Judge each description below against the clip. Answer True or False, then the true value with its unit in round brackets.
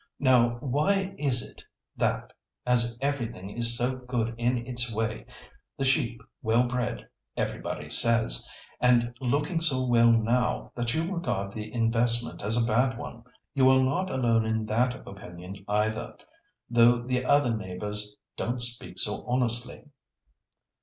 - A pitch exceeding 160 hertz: False (120 Hz)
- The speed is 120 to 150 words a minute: True (140 wpm)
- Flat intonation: True (2.0 semitones)